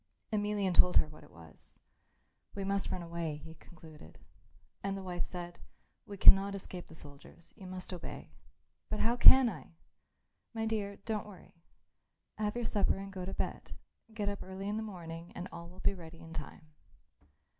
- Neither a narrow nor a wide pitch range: Yes, average, 3.4 semitones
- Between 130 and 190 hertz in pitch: Yes, medium, 185 Hz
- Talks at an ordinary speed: Yes, average, 175 wpm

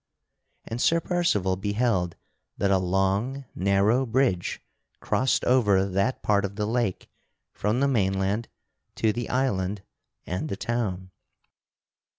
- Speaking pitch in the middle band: No, low, 105 Hz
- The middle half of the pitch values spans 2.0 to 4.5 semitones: Yes, average, 4.1 semitones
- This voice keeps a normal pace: No, slow, 125 wpm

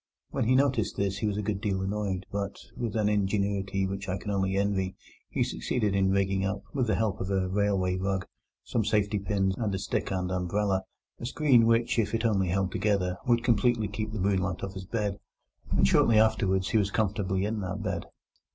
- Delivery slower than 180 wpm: No, fast, 205 wpm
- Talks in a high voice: No, low, 100 Hz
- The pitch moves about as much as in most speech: No, narrow, 2.0 semitones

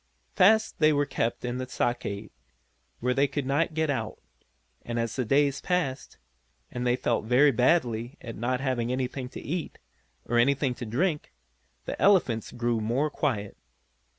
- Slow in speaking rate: No, average, 160 wpm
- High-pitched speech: No, low, 130 Hz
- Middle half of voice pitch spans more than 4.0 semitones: No, average, 3.4 semitones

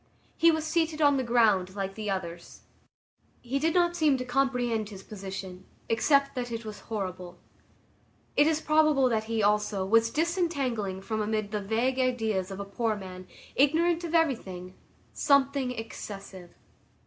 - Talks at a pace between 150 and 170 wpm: Yes, average, 155 wpm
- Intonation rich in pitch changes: Yes, wide, 6.0 semitones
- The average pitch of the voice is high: Yes, high, 230 Hz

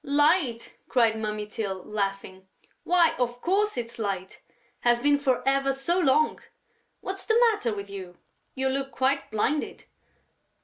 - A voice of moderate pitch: No, very high, 250 Hz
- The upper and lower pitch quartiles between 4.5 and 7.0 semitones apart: Yes, wide, 5.5 semitones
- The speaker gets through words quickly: No, average, 140 wpm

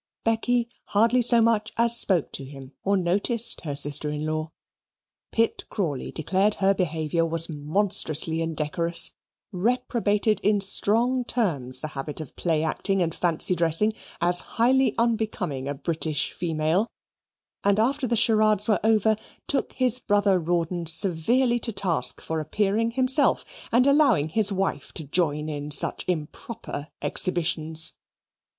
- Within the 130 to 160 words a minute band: Yes, average, 140 wpm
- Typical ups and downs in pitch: No, wide, 6.2 semitones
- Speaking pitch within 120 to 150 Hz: No, medium, 185 Hz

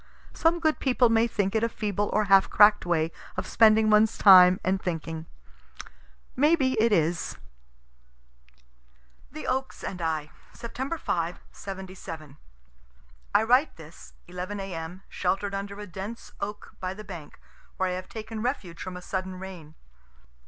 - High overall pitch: Yes, high, 195 Hz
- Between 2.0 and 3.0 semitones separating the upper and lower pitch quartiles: No, average, 3.7 semitones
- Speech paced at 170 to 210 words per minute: No, average, 150 wpm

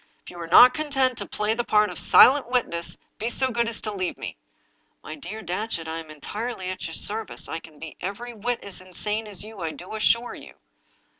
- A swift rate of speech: Yes, fast, 220 wpm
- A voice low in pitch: No, high, 210 Hz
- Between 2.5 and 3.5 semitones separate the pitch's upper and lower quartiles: No, average, 5.2 semitones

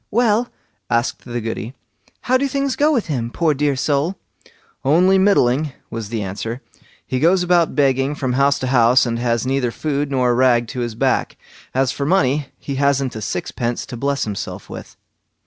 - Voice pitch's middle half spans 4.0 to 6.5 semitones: Yes, average, 4.3 semitones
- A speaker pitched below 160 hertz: Yes, low, 135 Hz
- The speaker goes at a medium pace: Yes, average, 180 wpm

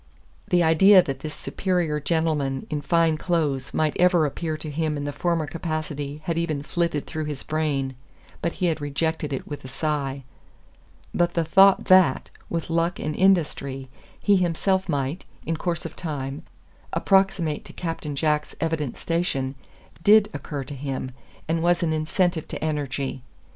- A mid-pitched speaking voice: Yes, medium, 155 Hz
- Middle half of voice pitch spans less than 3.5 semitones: Yes, average, 2.9 semitones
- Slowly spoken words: No, average, 160 wpm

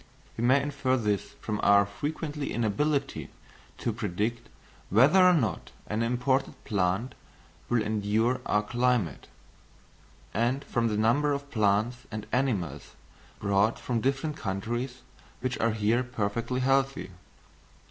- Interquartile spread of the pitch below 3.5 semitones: No, average, 3.9 semitones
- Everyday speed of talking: No, slow, 125 wpm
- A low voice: Yes, low, 120 Hz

